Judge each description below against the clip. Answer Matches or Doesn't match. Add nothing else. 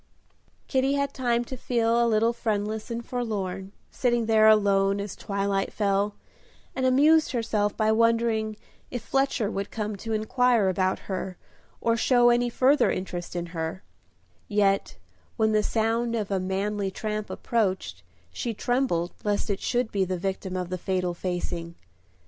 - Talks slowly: Doesn't match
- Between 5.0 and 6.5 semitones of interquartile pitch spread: Doesn't match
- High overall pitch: Matches